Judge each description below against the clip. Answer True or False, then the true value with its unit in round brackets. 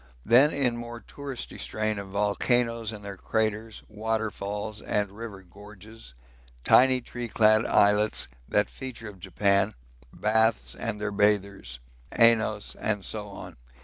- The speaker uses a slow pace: True (130 wpm)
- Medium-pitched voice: False (105 Hz)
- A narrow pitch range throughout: True (2.1 semitones)